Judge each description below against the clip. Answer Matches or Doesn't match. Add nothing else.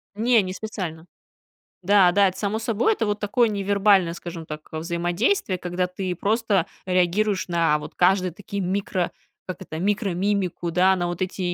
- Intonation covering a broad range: Doesn't match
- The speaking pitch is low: Doesn't match